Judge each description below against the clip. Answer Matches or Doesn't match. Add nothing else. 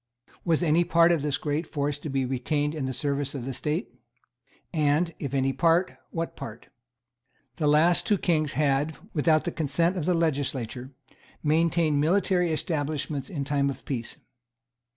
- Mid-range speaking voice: Matches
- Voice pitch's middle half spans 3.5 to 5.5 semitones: Doesn't match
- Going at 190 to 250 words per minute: Doesn't match